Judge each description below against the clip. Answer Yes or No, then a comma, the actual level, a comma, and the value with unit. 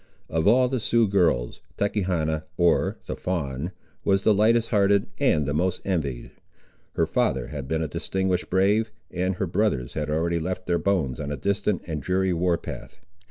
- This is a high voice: No, very low, 90 Hz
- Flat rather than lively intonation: No, average, 4.2 semitones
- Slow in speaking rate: No, average, 175 wpm